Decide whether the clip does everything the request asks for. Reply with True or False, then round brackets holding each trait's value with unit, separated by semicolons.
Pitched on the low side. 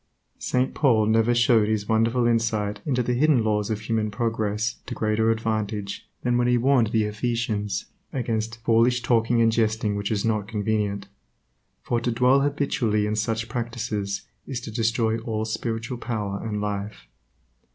True (115 Hz)